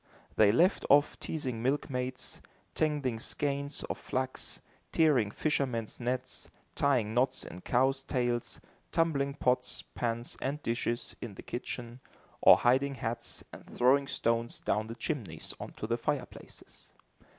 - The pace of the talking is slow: Yes, slow, 130 wpm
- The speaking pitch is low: Yes, low, 125 Hz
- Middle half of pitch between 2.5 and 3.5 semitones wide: Yes, average, 3.0 semitones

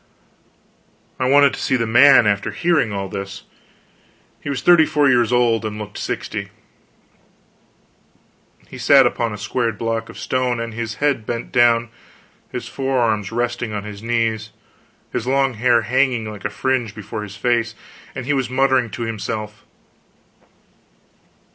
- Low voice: Yes, low, 115 Hz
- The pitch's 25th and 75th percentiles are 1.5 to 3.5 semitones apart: Yes, average, 3.0 semitones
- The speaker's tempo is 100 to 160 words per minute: Yes, average, 150 wpm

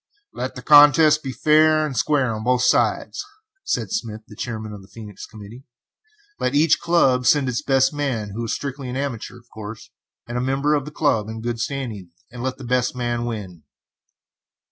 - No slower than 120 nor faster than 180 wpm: No, average, 190 wpm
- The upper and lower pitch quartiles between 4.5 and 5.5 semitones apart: No, average, 4.1 semitones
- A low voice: Yes, low, 125 Hz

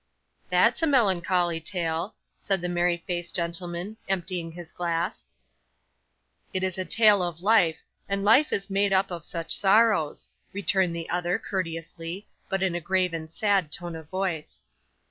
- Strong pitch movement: No, narrow, 2.5 semitones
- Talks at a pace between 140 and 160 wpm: Yes, average, 155 wpm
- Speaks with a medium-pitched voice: Yes, medium, 180 Hz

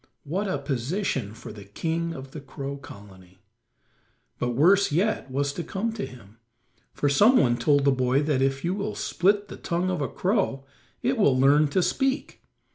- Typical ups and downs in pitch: No, wide, 6.5 semitones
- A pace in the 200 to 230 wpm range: No, average, 185 wpm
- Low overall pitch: No, medium, 145 Hz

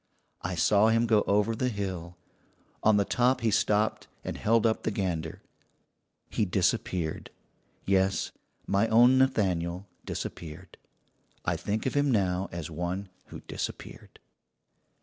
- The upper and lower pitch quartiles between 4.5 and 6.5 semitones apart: No, average, 3.8 semitones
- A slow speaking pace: Yes, slow, 130 wpm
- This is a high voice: No, low, 100 Hz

